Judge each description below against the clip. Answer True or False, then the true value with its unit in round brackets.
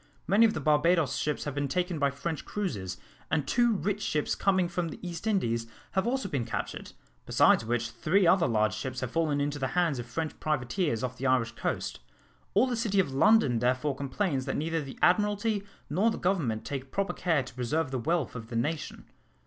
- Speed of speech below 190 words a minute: False (205 wpm)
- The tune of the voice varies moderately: False (6.4 semitones)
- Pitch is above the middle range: False (150 Hz)